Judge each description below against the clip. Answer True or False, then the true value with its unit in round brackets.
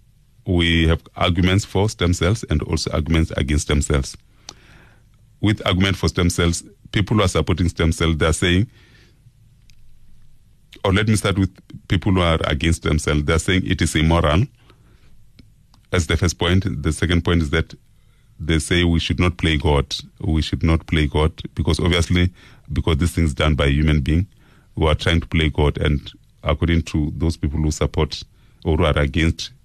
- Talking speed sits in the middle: True (175 wpm)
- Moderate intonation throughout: True (3.9 semitones)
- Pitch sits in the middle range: False (85 Hz)